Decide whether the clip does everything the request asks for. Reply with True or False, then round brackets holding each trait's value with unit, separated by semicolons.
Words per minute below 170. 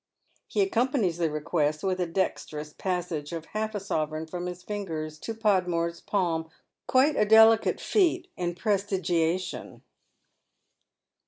True (135 wpm)